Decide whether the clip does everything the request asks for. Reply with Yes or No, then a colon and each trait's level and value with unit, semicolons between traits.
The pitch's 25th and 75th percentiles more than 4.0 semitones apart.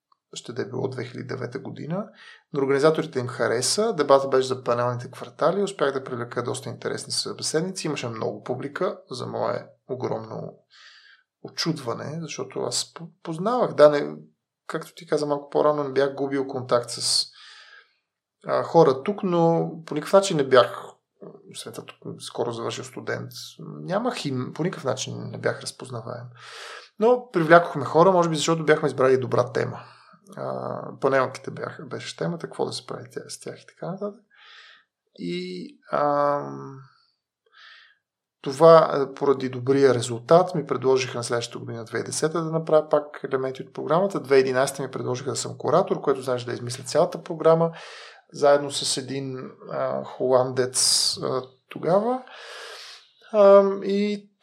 Yes: average, 4.6 semitones